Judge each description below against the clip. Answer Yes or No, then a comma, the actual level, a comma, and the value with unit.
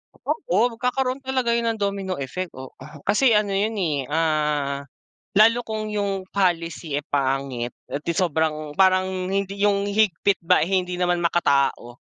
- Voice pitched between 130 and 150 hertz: No, medium, 185 Hz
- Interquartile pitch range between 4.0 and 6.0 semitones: Yes, average, 5.3 semitones